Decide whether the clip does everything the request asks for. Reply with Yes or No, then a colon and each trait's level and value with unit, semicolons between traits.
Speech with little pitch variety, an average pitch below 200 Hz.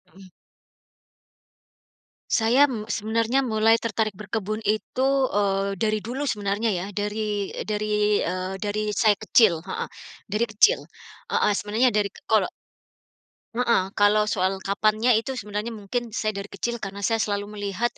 No: narrow, 1.9 semitones; high, 215 Hz